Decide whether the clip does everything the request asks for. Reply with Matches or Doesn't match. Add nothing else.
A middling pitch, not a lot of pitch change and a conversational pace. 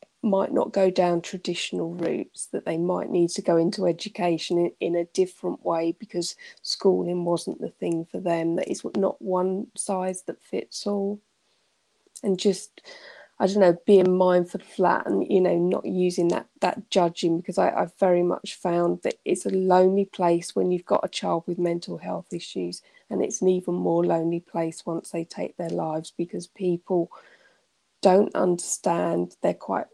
Matches